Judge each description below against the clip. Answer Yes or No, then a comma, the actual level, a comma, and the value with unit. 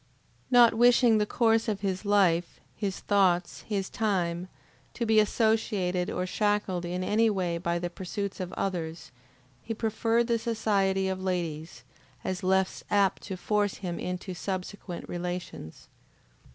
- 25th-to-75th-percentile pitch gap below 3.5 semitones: Yes, average, 3.1 semitones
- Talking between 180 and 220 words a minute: No, average, 140 wpm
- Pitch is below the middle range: No, high, 190 Hz